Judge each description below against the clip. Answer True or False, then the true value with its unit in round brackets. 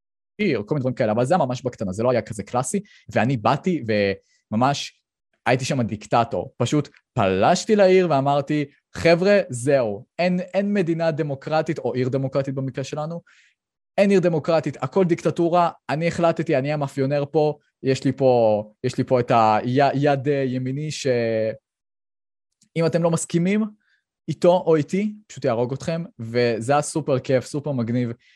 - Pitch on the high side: False (140 Hz)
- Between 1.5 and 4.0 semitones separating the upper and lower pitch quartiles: False (5.1 semitones)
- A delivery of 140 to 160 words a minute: True (145 wpm)